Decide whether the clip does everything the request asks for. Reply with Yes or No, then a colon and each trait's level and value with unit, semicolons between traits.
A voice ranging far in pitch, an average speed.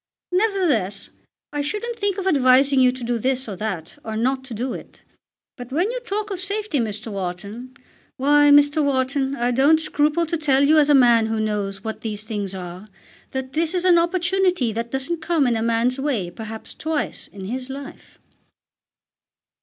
Yes: wide, 6.0 semitones; average, 185 wpm